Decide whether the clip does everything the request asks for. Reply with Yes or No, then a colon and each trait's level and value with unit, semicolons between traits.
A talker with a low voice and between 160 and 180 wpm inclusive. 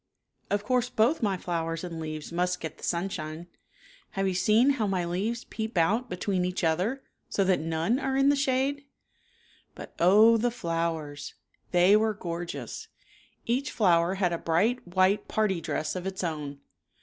No: medium, 185 Hz; average, 170 wpm